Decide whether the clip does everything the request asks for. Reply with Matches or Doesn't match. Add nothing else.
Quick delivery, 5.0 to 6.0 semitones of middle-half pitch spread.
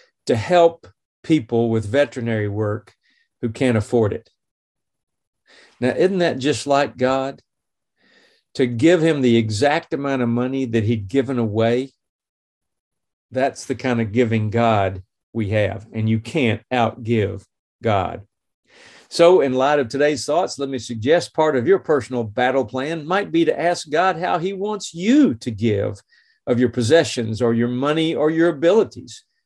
Doesn't match